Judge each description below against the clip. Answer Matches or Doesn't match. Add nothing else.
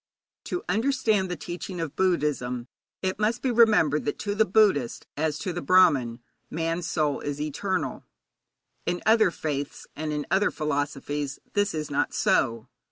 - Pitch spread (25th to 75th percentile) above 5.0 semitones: Matches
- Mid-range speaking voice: Matches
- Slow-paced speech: Doesn't match